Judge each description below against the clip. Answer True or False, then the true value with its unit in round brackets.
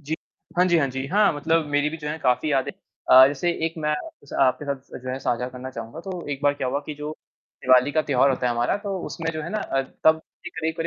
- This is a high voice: False (145 Hz)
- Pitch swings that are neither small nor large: True (3.5 semitones)